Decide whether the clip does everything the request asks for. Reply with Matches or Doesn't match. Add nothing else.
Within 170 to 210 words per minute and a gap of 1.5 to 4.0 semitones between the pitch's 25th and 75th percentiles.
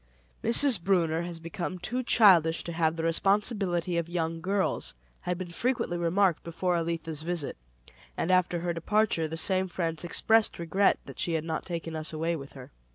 Matches